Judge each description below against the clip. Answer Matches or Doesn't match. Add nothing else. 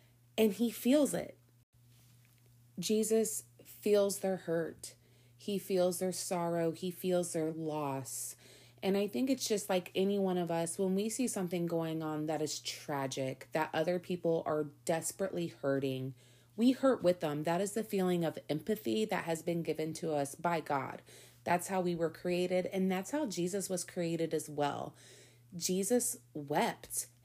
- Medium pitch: Matches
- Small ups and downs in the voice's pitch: Doesn't match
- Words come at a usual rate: Matches